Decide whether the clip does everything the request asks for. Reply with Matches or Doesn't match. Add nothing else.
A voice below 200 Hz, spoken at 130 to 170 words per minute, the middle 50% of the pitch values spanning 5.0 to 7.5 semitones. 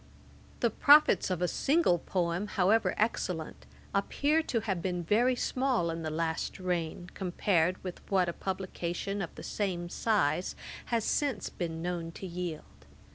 Doesn't match